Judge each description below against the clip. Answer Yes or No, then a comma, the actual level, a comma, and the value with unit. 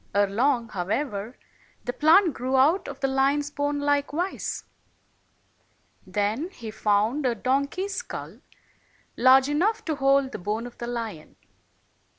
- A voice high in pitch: Yes, very high, 270 Hz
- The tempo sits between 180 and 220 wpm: No, average, 140 wpm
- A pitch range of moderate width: Yes, average, 4.3 semitones